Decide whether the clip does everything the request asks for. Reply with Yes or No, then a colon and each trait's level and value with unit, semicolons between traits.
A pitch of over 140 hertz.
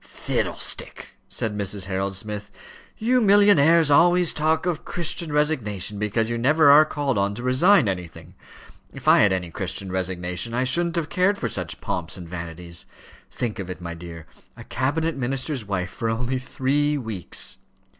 No: low, 115 Hz